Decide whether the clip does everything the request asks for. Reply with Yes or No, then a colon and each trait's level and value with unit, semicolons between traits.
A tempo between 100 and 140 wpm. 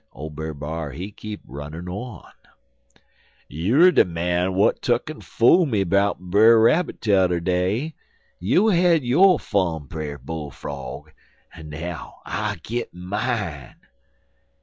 Yes: slow, 135 wpm